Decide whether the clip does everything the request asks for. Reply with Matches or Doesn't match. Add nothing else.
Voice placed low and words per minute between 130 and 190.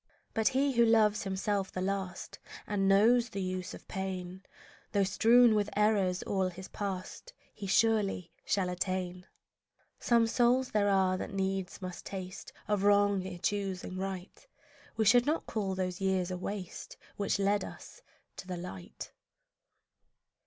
Doesn't match